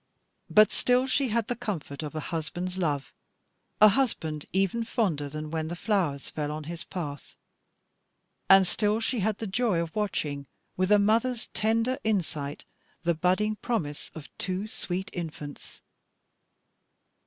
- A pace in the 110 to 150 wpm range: Yes, average, 145 wpm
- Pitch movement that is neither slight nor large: No, wide, 5.7 semitones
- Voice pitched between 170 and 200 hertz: Yes, medium, 185 Hz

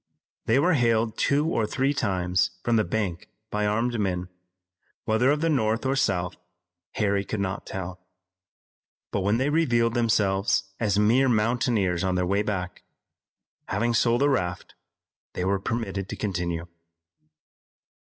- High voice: No, low, 105 Hz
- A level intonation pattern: No, average, 3.9 semitones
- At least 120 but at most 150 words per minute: Yes, average, 145 wpm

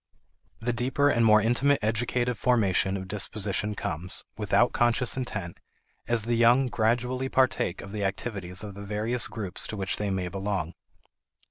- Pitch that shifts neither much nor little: Yes, average, 3.7 semitones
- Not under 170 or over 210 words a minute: No, average, 155 wpm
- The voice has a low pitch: Yes, low, 110 Hz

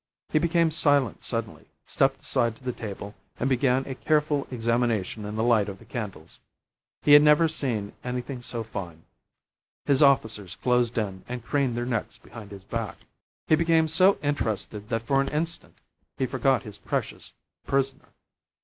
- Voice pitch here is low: Yes, low, 125 Hz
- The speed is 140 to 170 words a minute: Yes, average, 165 wpm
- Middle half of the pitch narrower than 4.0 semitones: No, average, 4.7 semitones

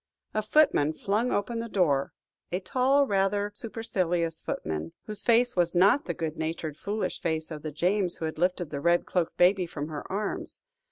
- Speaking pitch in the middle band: Yes, medium, 180 Hz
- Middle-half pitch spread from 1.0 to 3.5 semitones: No, average, 4.7 semitones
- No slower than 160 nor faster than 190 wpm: Yes, average, 180 wpm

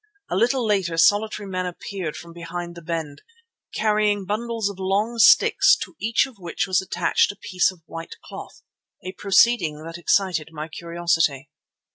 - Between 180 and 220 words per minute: No, average, 160 wpm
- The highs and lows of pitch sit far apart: No, average, 3.9 semitones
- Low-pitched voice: No, medium, 185 Hz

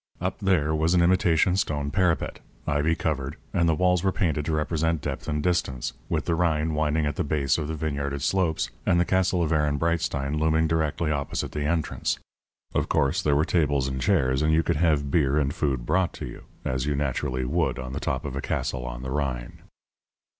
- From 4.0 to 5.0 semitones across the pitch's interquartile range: No, average, 2.9 semitones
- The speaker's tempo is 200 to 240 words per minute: Yes, fast, 205 wpm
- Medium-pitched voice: No, very low, 75 Hz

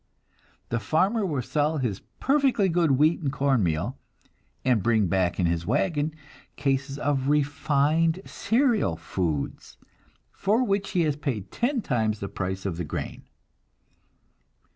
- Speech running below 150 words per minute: Yes, average, 140 wpm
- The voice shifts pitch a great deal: Yes, wide, 8.0 semitones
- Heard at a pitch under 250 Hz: Yes, medium, 140 Hz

